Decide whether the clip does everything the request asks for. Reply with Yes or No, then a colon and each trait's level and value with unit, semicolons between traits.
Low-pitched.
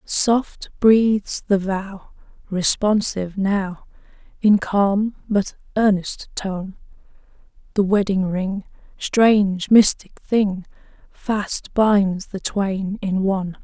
No: high, 200 Hz